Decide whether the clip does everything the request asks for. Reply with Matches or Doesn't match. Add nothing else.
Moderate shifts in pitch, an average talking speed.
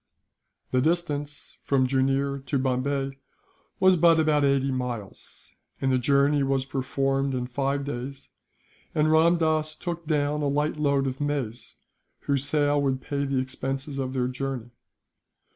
Doesn't match